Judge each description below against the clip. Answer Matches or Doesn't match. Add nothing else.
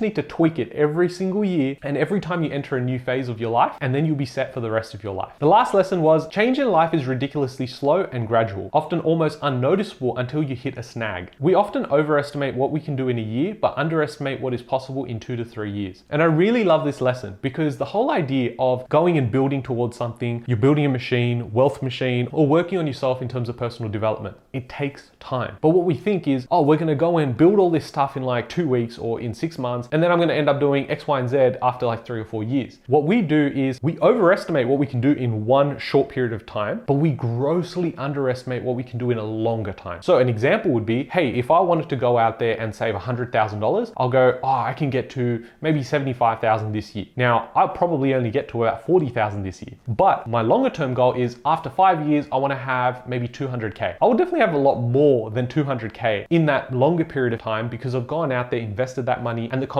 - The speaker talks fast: Matches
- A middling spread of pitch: Matches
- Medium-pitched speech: Doesn't match